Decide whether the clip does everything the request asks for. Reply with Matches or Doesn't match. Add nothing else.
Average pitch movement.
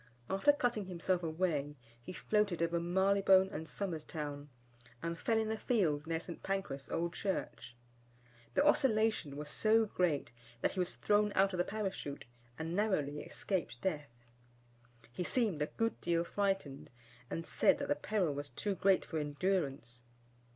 Matches